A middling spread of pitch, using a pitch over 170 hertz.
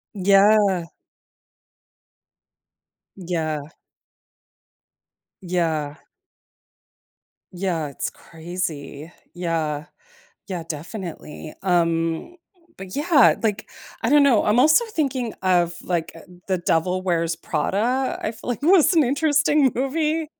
No: wide, 7.8 semitones; medium, 185 Hz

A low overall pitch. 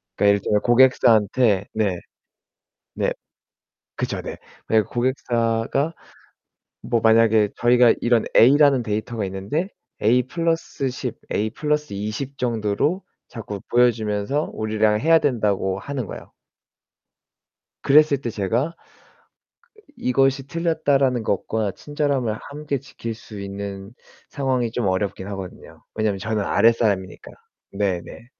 Yes: low, 115 Hz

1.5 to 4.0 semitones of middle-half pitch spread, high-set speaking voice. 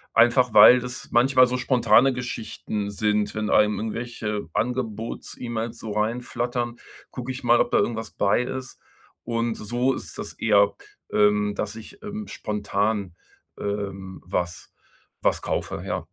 No: average, 2.9 semitones; low, 115 Hz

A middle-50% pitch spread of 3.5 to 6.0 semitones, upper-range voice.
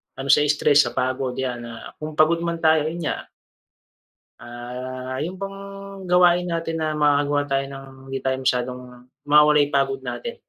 No: average, 3.9 semitones; medium, 145 Hz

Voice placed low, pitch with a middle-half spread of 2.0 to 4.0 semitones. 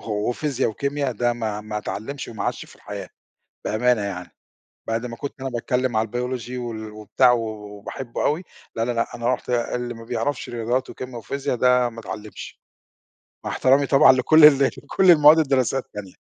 Yes: low, 120 Hz; average, 3.0 semitones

